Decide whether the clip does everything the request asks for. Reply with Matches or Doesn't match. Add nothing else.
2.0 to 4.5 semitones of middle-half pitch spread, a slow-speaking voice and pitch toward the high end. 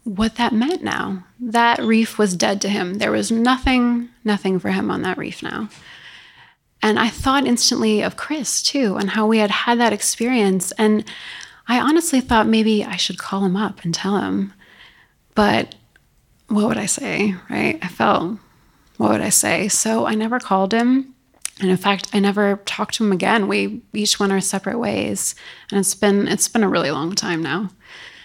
Doesn't match